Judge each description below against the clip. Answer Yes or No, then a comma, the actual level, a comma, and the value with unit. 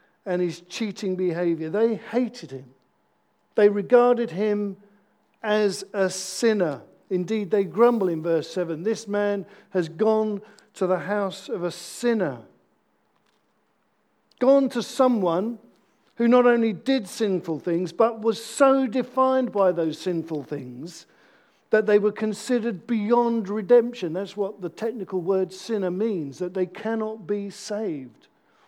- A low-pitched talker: No, high, 205 Hz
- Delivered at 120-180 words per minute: Yes, slow, 135 wpm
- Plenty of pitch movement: No, average, 4.0 semitones